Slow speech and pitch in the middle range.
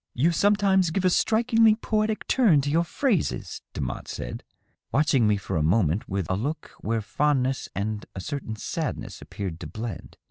No: average, 170 wpm; medium, 145 Hz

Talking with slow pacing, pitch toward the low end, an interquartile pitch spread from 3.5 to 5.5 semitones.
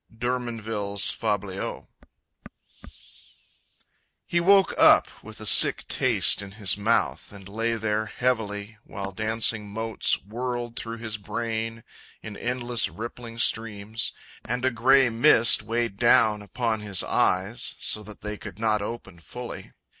No: slow, 130 wpm; low, 110 Hz; narrow, 2.4 semitones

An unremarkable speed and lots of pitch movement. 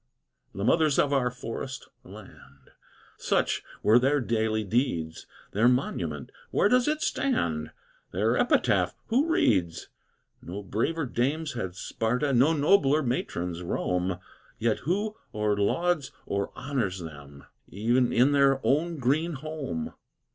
No: slow, 125 wpm; wide, 7.2 semitones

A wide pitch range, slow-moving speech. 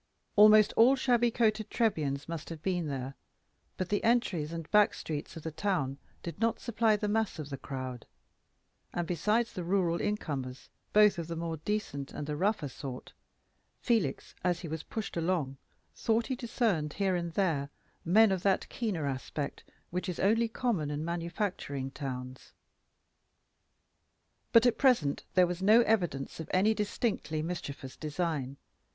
No: wide, 6.2 semitones; average, 160 wpm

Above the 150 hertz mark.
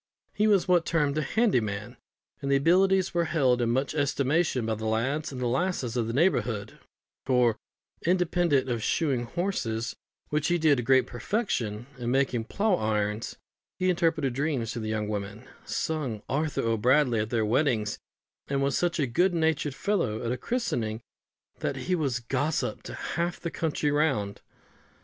No: low, 135 Hz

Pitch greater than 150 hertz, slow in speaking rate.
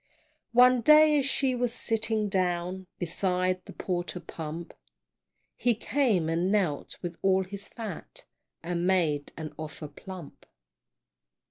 Yes: medium, 185 Hz; slow, 125 wpm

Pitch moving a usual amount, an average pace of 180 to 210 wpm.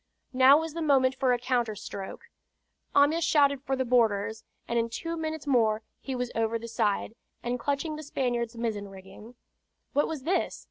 Yes: average, 4.0 semitones; average, 185 wpm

